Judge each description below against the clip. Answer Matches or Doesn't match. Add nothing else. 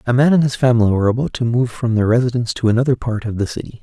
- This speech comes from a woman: Doesn't match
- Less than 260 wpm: Doesn't match